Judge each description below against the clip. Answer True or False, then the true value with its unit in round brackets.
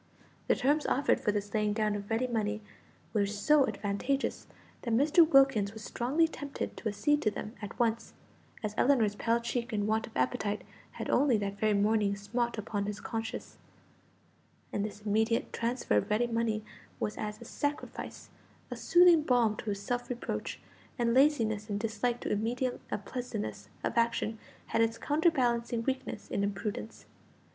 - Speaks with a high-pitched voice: True (225 Hz)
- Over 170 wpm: False (165 wpm)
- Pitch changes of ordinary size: True (3.0 semitones)